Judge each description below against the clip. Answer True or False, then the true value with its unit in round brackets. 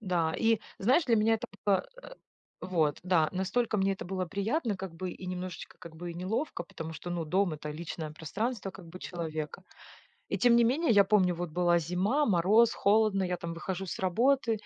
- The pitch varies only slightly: False (4.1 semitones)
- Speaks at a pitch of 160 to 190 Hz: True (185 Hz)